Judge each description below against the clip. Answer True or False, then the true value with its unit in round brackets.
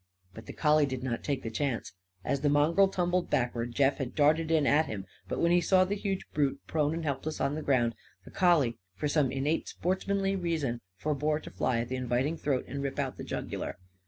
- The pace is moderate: False (215 wpm)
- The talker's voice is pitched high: False (145 Hz)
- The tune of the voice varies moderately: True (4.0 semitones)